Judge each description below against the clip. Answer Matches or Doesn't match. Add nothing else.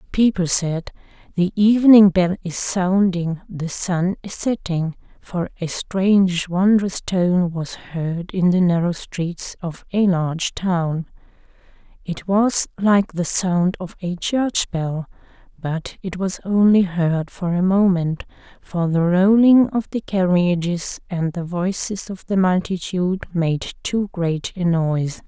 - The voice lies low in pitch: Doesn't match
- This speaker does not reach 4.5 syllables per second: Matches